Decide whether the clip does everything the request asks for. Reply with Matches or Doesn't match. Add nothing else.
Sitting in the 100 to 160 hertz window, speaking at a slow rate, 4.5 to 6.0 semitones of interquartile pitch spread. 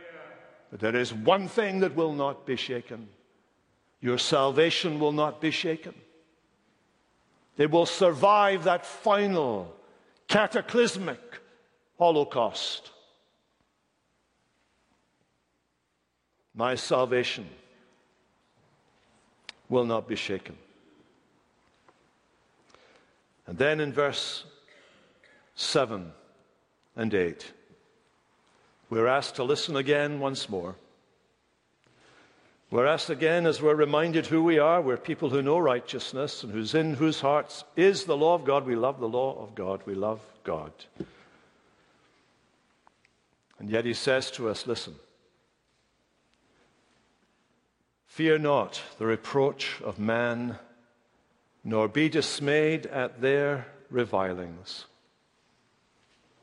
Matches